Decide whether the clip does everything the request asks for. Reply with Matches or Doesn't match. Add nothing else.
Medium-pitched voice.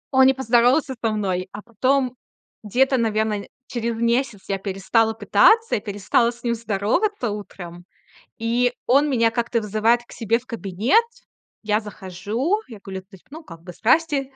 Doesn't match